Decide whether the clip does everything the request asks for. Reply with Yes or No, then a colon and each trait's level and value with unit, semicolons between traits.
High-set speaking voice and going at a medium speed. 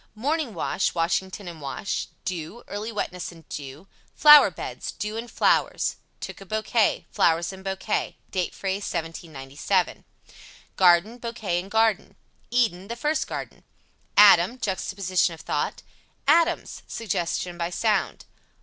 No: high, 195 Hz; slow, 130 wpm